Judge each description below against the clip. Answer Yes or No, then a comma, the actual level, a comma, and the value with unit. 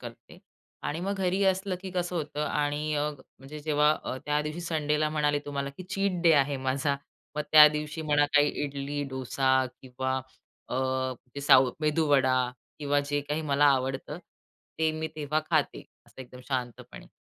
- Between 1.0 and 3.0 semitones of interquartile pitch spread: Yes, narrow, 2.5 semitones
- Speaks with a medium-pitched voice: Yes, medium, 145 Hz